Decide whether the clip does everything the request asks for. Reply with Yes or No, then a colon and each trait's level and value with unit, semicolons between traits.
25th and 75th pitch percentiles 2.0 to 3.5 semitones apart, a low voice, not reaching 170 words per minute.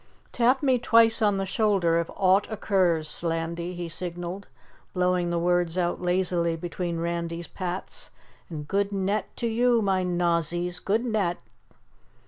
No: average, 2.8 semitones; medium, 180 Hz; average, 140 wpm